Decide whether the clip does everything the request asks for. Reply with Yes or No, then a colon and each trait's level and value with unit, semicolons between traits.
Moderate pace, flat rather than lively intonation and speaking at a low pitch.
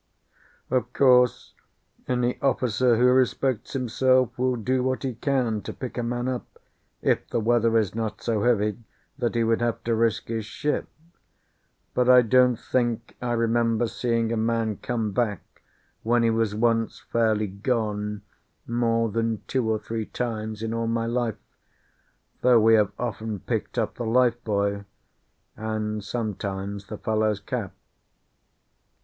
Yes: average, 150 wpm; narrow, 2.1 semitones; low, 115 Hz